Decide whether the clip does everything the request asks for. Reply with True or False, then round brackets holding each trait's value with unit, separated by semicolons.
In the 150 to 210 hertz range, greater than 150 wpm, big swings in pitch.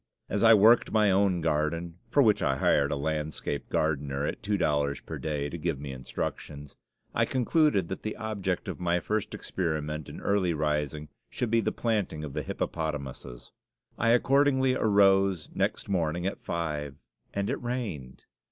False (85 Hz; 165 wpm; 5.8 semitones)